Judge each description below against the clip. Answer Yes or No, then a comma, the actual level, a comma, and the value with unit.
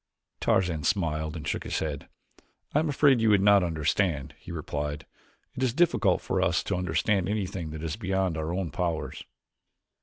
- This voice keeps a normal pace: Yes, average, 175 wpm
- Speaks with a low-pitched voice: Yes, very low, 90 Hz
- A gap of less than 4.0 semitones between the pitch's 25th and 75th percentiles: No, average, 4.4 semitones